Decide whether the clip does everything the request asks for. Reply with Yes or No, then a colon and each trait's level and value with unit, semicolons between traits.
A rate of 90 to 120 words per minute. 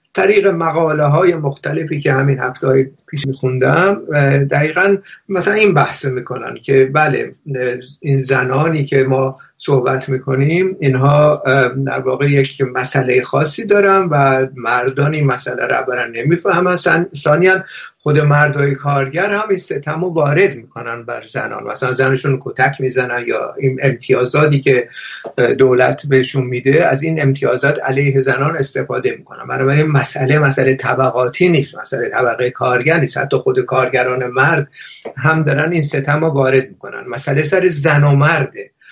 No: average, 145 wpm